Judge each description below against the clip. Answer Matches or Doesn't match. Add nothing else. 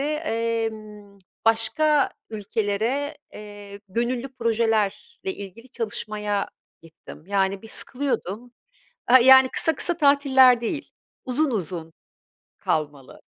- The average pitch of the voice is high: Matches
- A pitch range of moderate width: Matches